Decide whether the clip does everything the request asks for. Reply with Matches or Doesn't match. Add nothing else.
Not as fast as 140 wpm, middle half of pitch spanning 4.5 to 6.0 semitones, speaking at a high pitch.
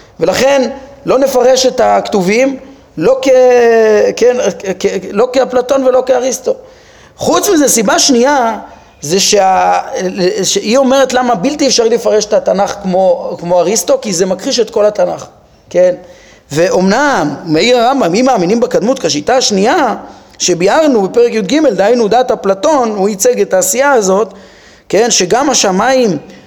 Matches